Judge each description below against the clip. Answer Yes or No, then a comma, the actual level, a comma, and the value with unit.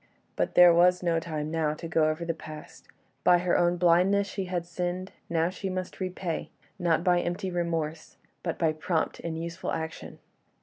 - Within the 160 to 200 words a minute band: Yes, average, 180 wpm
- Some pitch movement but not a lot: No, narrow, 1.8 semitones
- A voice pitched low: No, medium, 170 Hz